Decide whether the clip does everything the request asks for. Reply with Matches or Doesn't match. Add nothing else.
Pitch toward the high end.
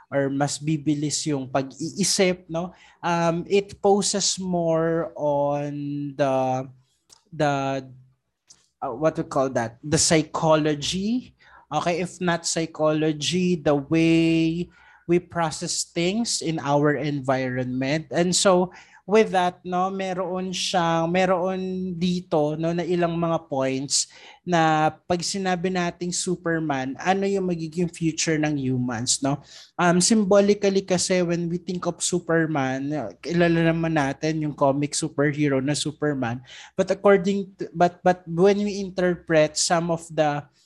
Doesn't match